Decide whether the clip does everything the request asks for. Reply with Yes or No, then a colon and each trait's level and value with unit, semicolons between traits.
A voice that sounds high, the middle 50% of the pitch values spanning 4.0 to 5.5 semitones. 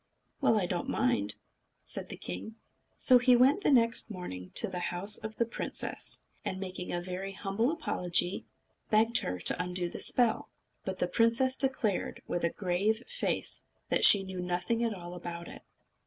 Yes: high, 195 Hz; average, 4.6 semitones